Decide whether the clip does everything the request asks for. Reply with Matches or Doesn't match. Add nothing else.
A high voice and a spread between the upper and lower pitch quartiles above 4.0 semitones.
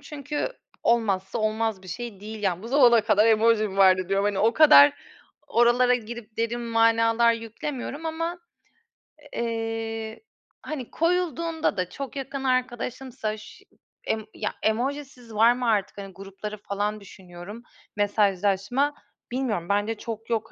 Doesn't match